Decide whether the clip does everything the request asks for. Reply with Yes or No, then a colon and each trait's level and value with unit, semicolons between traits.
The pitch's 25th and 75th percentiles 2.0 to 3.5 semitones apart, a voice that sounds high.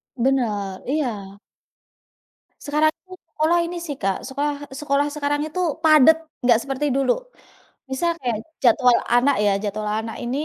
No: average, 4.3 semitones; very high, 270 Hz